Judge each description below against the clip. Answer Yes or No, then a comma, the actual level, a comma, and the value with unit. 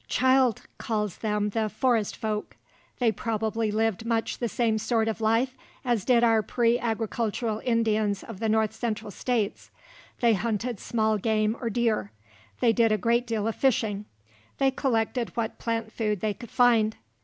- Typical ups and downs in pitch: No, narrow, 1.7 semitones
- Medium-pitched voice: No, high, 225 Hz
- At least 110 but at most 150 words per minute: No, average, 165 wpm